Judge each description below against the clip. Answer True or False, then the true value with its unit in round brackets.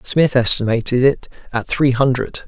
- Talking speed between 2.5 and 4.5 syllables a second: False (4.7 syllables/s)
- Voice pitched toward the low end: True (125 Hz)